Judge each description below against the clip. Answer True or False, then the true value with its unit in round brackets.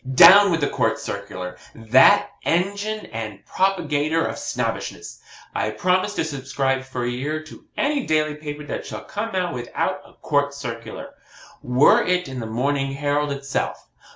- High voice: False (145 Hz)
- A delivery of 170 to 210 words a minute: False (155 wpm)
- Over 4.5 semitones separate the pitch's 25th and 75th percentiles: True (5.2 semitones)